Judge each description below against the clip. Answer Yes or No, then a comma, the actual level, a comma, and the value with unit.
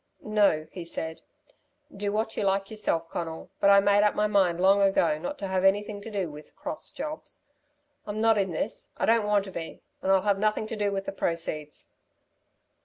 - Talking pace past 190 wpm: Yes, fast, 205 wpm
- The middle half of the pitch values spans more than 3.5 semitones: No, average, 2.9 semitones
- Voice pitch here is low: No, high, 200 Hz